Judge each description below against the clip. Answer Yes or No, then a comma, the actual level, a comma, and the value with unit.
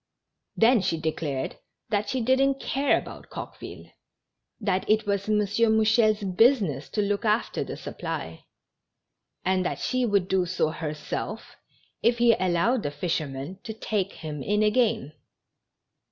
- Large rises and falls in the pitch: No, average, 4.1 semitones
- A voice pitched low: No, high, 205 Hz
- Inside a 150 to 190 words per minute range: No, average, 140 wpm